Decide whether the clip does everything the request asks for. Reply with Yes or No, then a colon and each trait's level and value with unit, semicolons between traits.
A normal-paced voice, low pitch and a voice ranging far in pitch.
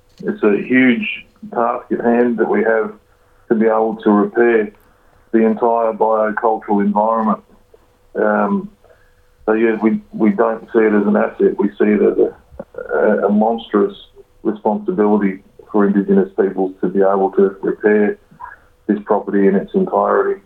No: average, 150 wpm; low, 110 Hz; narrow, 2.5 semitones